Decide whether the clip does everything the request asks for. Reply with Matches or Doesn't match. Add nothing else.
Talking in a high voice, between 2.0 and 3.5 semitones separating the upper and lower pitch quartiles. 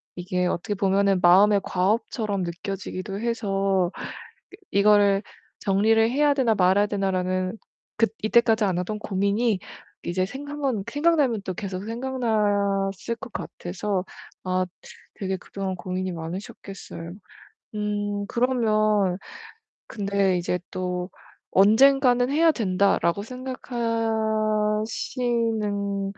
Matches